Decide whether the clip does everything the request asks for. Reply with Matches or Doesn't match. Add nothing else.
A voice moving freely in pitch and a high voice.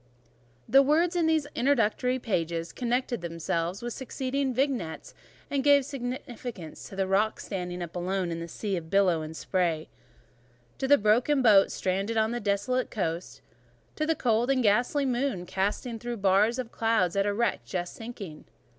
Matches